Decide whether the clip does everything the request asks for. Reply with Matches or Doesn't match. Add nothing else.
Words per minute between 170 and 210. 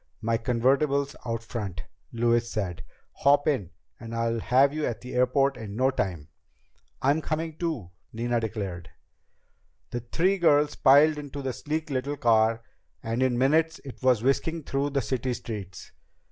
Doesn't match